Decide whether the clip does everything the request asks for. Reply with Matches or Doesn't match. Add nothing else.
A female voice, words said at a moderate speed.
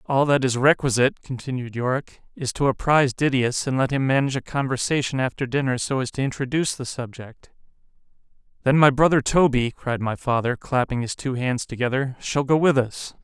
Doesn't match